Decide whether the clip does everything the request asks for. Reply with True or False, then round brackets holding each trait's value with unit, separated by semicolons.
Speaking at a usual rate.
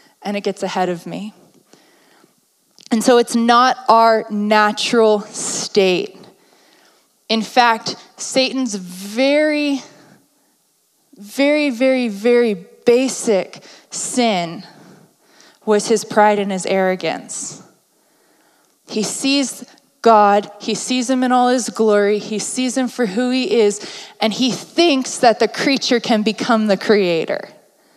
False (120 wpm)